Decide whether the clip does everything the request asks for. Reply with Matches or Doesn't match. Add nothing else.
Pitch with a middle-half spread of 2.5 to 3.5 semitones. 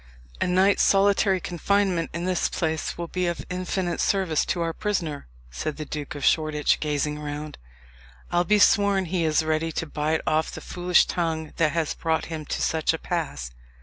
Matches